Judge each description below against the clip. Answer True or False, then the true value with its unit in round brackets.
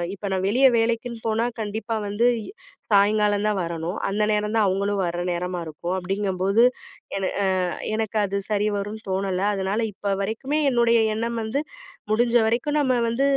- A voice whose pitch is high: True (210 Hz)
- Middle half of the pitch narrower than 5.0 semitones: True (2.8 semitones)